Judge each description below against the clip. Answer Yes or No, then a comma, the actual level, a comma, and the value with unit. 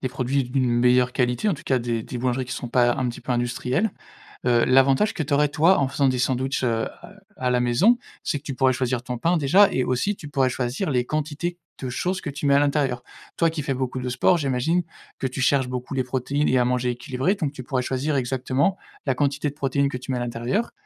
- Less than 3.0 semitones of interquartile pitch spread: Yes, narrow, 2.6 semitones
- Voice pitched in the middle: No, low, 130 Hz